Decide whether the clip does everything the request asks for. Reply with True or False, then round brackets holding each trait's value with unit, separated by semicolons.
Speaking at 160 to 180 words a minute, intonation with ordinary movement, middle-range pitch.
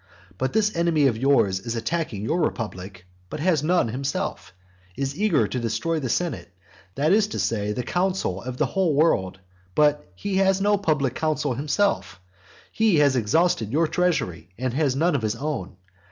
False (170 wpm; 6.8 semitones; 145 Hz)